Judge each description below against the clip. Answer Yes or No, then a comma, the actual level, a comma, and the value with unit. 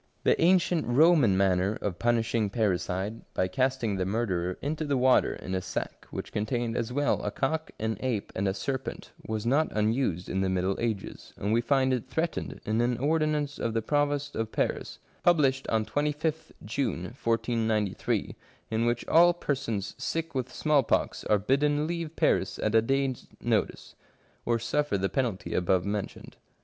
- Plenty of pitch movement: Yes, wide, 5.7 semitones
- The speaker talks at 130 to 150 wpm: No, average, 165 wpm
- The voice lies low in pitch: Yes, low, 120 Hz